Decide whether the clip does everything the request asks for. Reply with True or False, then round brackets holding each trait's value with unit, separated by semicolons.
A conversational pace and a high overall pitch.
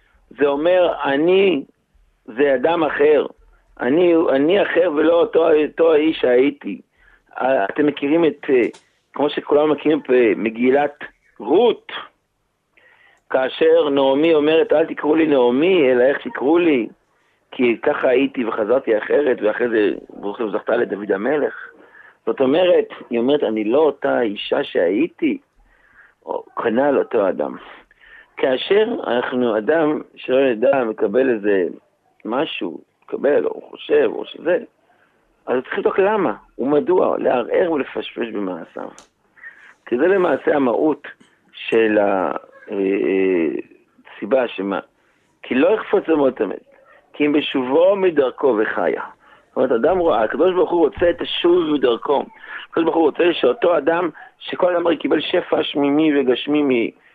True (130 wpm; 300 Hz)